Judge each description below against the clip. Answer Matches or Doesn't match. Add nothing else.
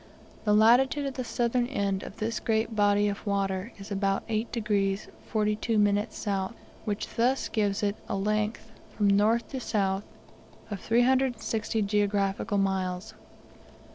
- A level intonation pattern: Matches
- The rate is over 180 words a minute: Doesn't match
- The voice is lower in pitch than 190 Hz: Doesn't match